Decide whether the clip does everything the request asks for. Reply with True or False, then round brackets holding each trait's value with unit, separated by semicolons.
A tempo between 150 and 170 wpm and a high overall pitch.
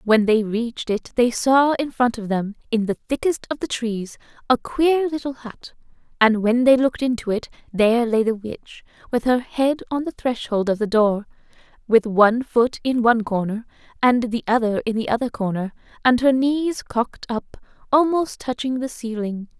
False (185 wpm; 235 Hz)